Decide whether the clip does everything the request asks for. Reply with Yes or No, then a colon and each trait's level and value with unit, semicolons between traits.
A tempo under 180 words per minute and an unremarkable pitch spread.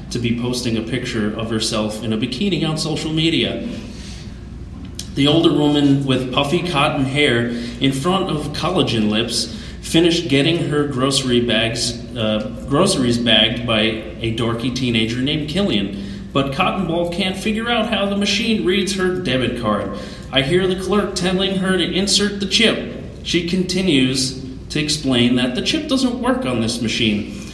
No: average, 160 wpm; wide, 7.8 semitones